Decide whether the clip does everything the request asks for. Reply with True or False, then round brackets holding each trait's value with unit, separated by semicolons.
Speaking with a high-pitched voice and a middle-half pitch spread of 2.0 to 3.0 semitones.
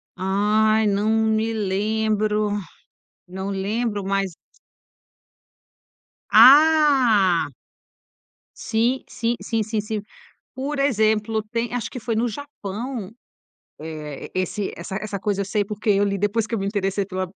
True (215 Hz; 2.5 semitones)